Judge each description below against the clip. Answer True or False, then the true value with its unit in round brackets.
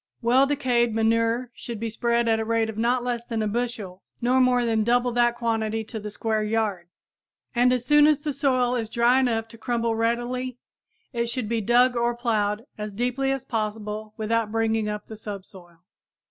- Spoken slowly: False (190 wpm)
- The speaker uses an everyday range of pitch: False (2.0 semitones)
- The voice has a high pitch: True (230 Hz)